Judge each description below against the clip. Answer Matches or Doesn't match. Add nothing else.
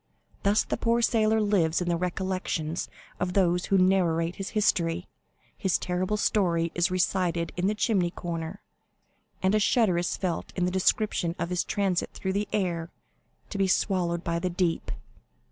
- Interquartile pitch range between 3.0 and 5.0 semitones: Doesn't match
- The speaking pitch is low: Doesn't match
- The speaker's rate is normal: Matches